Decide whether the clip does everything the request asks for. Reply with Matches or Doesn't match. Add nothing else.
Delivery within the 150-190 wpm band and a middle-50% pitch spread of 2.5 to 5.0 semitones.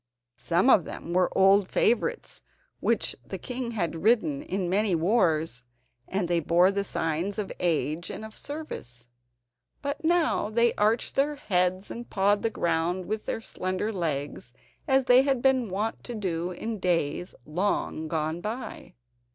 Doesn't match